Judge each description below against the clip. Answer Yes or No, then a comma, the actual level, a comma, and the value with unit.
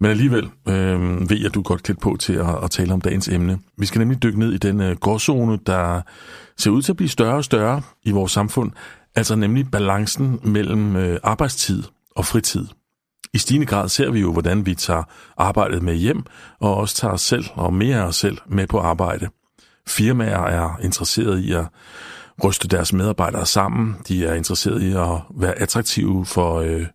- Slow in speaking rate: No, average, 195 wpm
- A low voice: Yes, low, 100 Hz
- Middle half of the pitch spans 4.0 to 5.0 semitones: No, average, 3.3 semitones